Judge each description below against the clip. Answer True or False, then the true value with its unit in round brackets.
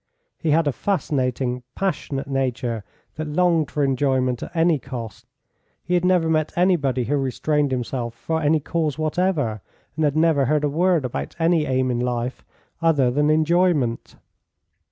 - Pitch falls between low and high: True (145 Hz)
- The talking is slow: False (155 wpm)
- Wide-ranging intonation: False (4.2 semitones)